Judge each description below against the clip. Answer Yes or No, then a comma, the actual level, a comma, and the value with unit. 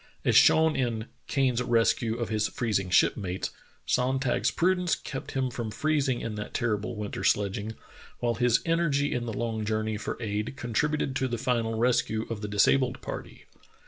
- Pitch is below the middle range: Yes, low, 120 Hz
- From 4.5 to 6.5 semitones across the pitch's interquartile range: No, average, 3.4 semitones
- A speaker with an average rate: Yes, average, 170 wpm